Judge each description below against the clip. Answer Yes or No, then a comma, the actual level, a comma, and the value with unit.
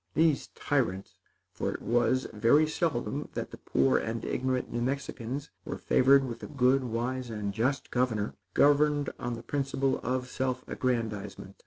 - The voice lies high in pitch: No, low, 125 Hz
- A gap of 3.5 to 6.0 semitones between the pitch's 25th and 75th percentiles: No, average, 3.1 semitones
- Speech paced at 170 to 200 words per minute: No, average, 155 wpm